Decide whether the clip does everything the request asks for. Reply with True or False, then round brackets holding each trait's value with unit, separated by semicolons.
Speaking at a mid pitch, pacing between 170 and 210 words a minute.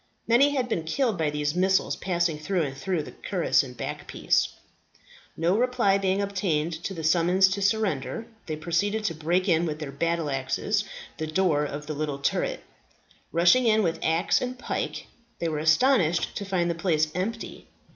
True (170 Hz; 175 wpm)